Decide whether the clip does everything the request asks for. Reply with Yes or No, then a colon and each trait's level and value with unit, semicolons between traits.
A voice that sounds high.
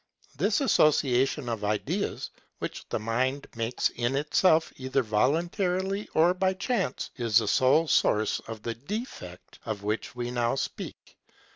No: low, 130 Hz